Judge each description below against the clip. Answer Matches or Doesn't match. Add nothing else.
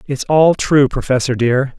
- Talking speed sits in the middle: Matches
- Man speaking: Matches